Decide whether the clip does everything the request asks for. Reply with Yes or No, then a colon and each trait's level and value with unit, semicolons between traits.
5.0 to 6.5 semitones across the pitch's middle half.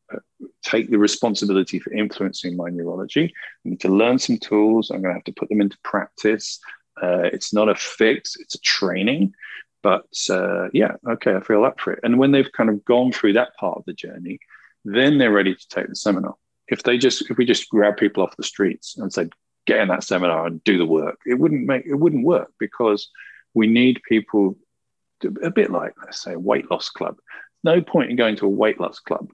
No: average, 3.4 semitones